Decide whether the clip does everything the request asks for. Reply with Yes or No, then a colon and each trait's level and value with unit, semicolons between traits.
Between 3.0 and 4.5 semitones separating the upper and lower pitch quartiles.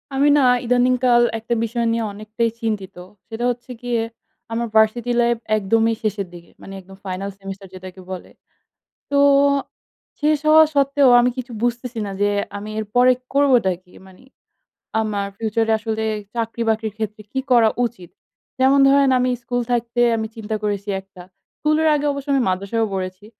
Yes: average, 3.3 semitones